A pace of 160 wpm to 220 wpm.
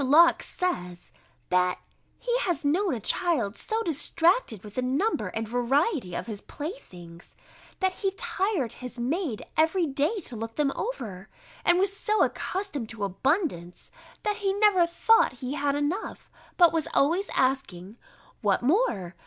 No: average, 150 wpm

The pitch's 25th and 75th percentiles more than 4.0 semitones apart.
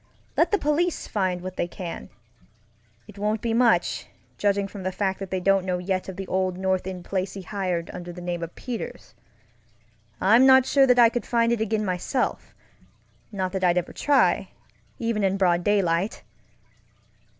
No: average, 3.5 semitones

